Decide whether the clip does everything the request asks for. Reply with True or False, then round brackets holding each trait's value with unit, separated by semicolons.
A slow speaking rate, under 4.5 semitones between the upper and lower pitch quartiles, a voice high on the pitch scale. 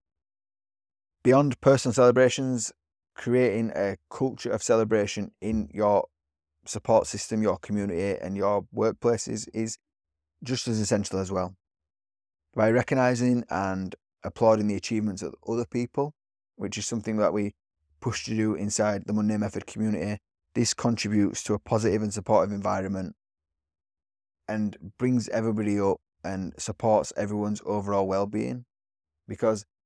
False (125 wpm; 2.9 semitones; 105 Hz)